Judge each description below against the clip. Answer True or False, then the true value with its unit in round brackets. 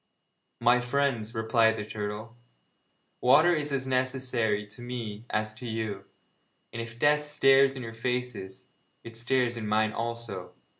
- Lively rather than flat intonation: False (2.9 semitones)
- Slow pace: False (145 wpm)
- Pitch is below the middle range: True (115 Hz)